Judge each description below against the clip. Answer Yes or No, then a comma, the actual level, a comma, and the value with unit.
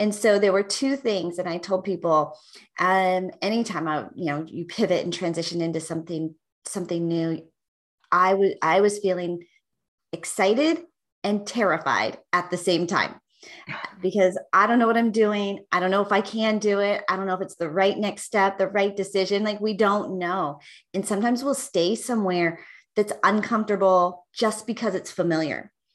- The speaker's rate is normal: Yes, average, 180 wpm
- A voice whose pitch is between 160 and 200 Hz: Yes, high, 190 Hz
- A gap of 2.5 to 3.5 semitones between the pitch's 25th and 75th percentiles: Yes, average, 3.1 semitones